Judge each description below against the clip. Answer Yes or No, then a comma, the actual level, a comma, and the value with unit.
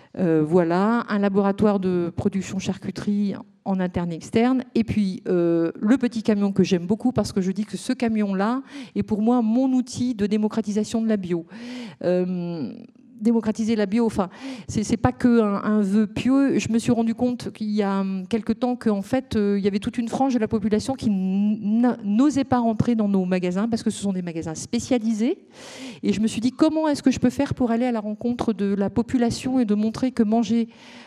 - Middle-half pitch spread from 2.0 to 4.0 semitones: Yes, average, 3.3 semitones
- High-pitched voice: Yes, high, 220 Hz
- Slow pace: No, average, 210 wpm